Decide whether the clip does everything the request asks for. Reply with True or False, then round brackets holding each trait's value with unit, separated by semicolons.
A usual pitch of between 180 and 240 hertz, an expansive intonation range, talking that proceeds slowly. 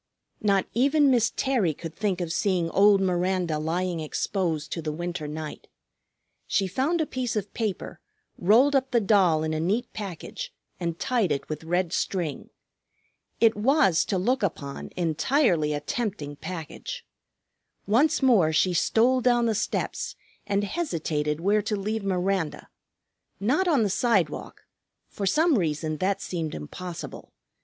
False (190 Hz; 6.0 semitones; 150 wpm)